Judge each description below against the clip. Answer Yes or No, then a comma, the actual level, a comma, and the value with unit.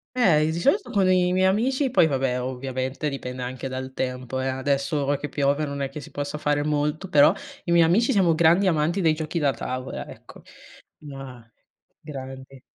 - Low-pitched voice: No, medium, 145 Hz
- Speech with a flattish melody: No, average, 4.3 semitones